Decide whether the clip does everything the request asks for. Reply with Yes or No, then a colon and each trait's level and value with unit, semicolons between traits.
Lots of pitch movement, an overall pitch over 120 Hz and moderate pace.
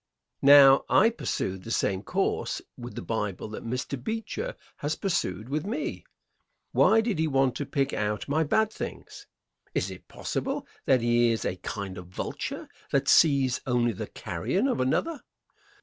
Yes: wide, 7.1 semitones; low, 135 Hz; average, 165 wpm